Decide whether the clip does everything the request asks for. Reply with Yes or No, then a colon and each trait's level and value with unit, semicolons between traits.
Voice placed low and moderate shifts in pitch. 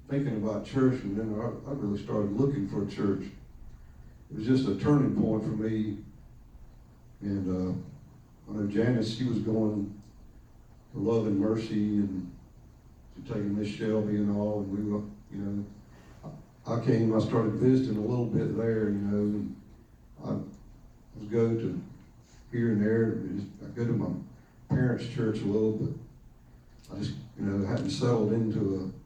No: low, 110 Hz; narrow, 2.2 semitones